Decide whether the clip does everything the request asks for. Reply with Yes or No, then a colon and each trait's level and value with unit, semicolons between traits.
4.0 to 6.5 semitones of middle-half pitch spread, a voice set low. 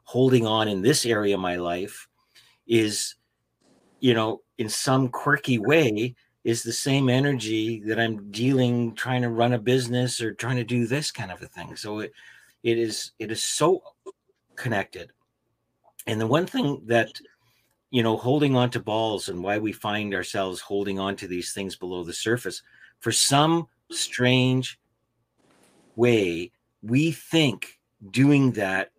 No: average, 3.3 semitones; low, 115 Hz